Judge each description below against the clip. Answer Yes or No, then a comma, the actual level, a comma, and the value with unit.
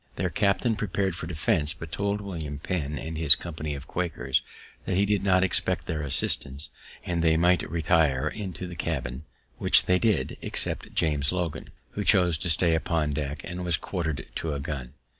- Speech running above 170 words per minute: Yes, average, 180 wpm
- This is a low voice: Yes, very low, 80 Hz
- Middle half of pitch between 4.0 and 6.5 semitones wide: No, average, 3.6 semitones